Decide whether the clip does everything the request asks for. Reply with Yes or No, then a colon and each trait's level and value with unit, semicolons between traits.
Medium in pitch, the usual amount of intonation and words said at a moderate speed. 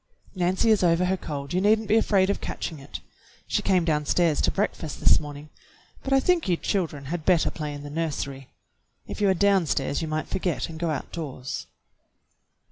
Yes: medium, 170 Hz; average, 4.2 semitones; average, 195 wpm